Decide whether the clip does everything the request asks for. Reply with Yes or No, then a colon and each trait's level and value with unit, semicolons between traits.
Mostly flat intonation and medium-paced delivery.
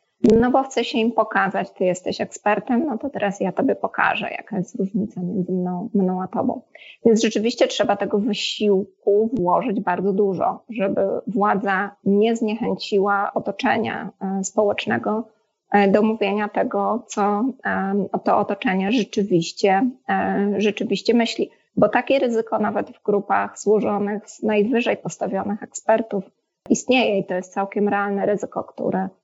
Yes: narrow, 2.2 semitones; average, 135 wpm